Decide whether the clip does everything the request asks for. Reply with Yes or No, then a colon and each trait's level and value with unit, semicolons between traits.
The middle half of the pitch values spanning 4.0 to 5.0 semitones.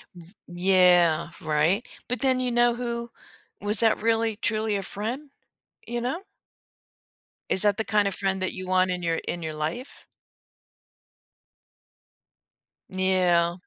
Yes: average, 4.6 semitones